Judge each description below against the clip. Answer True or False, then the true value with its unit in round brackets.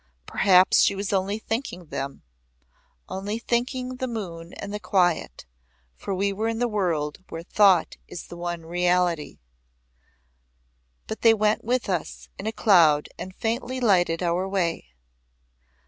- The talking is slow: False (145 wpm)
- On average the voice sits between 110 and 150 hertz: False (190 Hz)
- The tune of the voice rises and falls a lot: False (4.2 semitones)